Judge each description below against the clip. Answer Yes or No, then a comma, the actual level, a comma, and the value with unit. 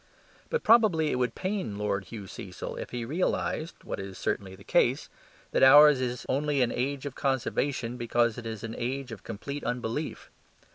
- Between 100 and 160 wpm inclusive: No, average, 180 wpm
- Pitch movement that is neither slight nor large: Yes, average, 4.2 semitones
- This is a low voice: Yes, low, 125 Hz